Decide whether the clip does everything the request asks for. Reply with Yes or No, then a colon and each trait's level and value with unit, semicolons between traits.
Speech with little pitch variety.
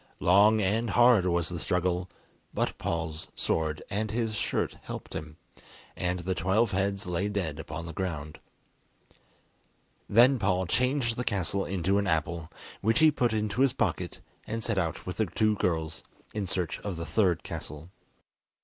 No: average, 4.2 semitones